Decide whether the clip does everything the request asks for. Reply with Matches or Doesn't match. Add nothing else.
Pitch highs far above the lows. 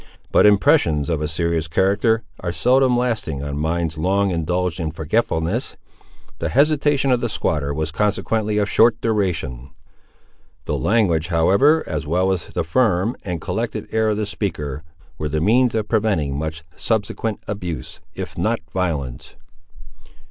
Matches